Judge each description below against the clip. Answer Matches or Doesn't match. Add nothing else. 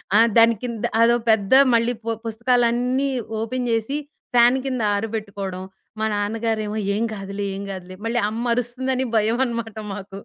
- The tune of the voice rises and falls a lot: Doesn't match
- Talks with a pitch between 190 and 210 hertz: Doesn't match